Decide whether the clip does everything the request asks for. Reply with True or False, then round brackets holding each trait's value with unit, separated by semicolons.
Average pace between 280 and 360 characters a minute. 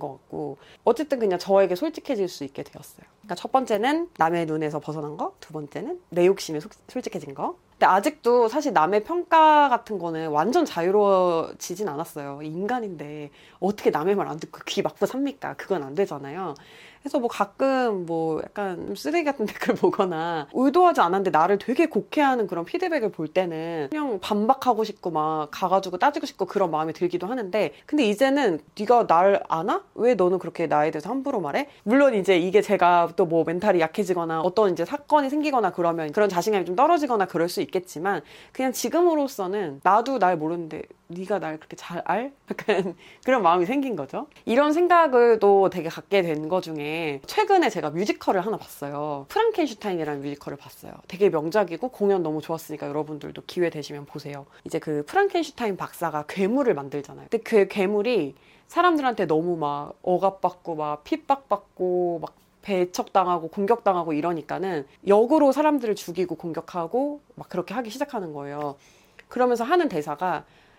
False (385 characters per minute)